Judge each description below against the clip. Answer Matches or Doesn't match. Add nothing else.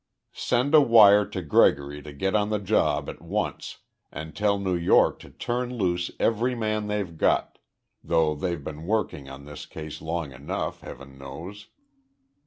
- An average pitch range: Doesn't match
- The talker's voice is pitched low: Matches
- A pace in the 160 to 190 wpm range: Matches